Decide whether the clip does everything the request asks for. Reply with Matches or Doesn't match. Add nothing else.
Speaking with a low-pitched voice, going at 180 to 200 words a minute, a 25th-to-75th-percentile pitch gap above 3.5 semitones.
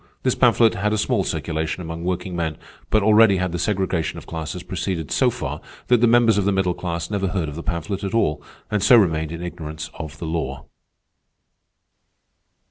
Matches